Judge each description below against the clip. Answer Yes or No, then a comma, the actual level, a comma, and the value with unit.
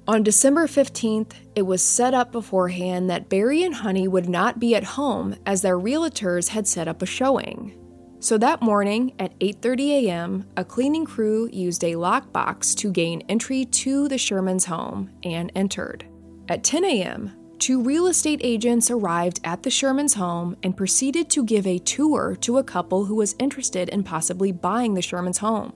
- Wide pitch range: Yes, wide, 5.8 semitones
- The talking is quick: No, average, 175 wpm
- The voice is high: Yes, high, 205 Hz